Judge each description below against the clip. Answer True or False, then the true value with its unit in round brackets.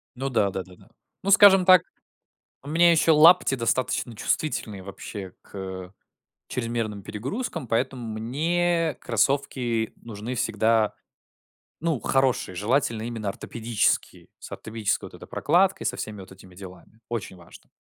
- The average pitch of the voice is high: False (115 Hz)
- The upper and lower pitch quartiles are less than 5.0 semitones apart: False (5.7 semitones)